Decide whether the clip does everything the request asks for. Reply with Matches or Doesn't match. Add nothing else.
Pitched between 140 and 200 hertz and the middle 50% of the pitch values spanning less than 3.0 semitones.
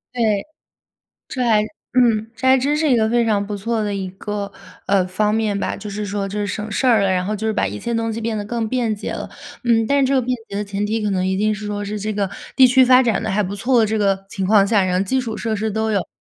Doesn't match